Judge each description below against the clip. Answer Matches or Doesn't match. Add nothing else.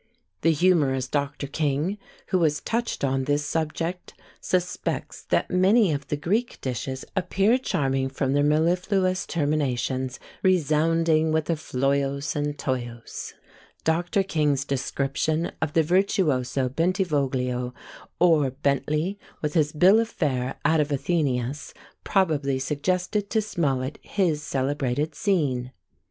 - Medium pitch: Matches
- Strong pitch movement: Doesn't match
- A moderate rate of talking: Doesn't match